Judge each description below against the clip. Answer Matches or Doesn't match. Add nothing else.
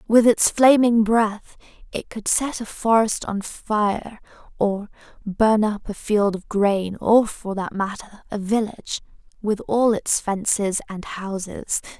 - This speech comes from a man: Doesn't match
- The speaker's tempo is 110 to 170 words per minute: Matches